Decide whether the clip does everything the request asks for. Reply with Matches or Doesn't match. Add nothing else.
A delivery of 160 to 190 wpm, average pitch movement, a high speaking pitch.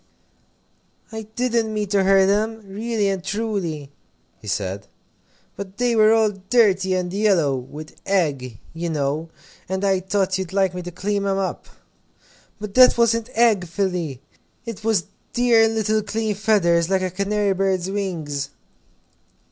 Doesn't match